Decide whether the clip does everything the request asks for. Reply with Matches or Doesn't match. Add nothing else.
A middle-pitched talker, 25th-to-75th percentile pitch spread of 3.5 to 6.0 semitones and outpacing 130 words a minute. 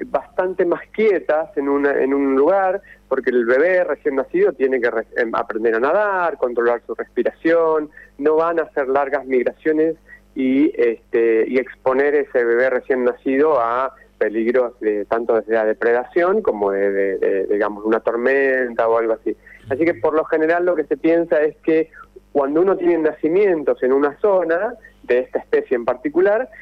Matches